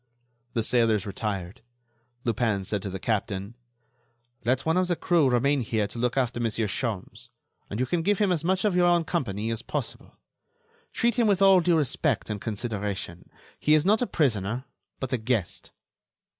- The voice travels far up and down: Yes, wide, 7.9 semitones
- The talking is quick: No, average, 180 wpm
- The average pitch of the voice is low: Yes, low, 120 Hz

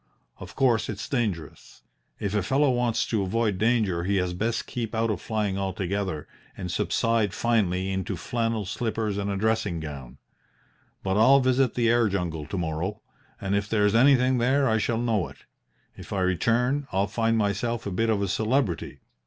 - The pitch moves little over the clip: No, average, 3.4 semitones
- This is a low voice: Yes, low, 105 Hz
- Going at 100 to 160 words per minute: No, average, 180 wpm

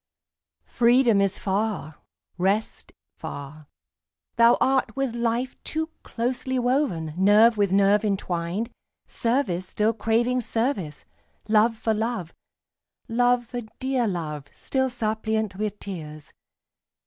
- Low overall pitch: No, high, 220 Hz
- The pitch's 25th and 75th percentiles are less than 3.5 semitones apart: No, average, 4.1 semitones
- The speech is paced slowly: Yes, slow, 110 wpm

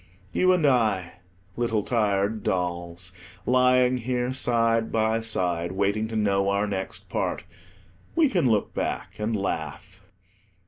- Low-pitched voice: Yes, low, 110 Hz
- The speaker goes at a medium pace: No, slow, 130 wpm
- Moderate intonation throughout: Yes, average, 3.9 semitones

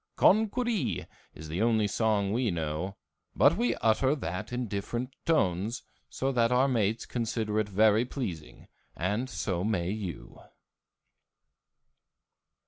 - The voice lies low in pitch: Yes, low, 110 Hz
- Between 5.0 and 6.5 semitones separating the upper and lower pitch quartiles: No, average, 4.4 semitones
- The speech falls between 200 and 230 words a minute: No, slow, 135 wpm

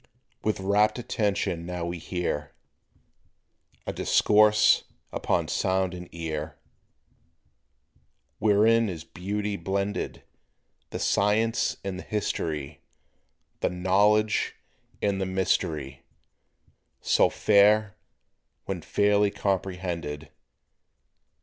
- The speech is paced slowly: Yes, slow, 85 wpm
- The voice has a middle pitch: No, very low, 95 Hz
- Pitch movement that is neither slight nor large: Yes, average, 3.3 semitones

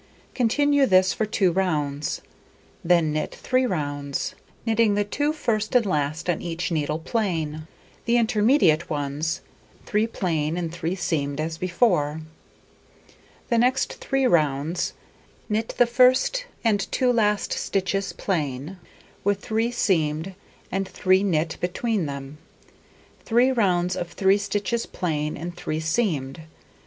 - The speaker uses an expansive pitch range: Yes, wide, 6.1 semitones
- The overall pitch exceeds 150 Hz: Yes, medium, 185 Hz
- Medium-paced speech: No, slow, 130 wpm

